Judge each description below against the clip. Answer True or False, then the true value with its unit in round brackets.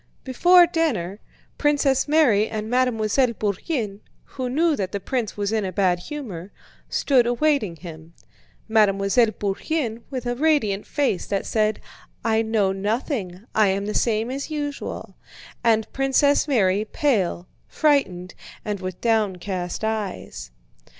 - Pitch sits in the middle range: False (220 Hz)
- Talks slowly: True (130 wpm)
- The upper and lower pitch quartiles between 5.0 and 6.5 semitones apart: True (5.4 semitones)